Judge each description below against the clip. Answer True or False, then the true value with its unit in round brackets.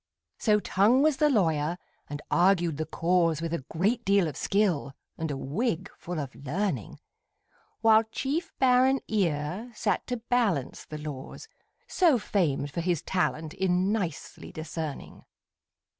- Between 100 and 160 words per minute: True (145 wpm)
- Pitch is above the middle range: False (180 Hz)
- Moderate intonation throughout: False (6.1 semitones)